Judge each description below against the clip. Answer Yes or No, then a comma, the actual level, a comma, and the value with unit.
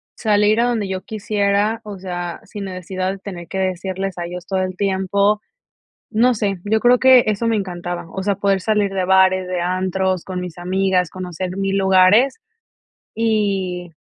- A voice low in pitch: No, high, 190 Hz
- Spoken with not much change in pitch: Yes, narrow, 2.0 semitones